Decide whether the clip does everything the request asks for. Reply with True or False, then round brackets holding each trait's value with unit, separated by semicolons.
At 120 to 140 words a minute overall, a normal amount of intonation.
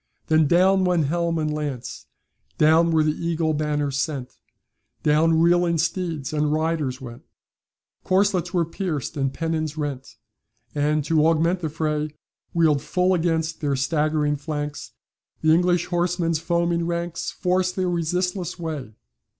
False (135 wpm; 2.3 semitones)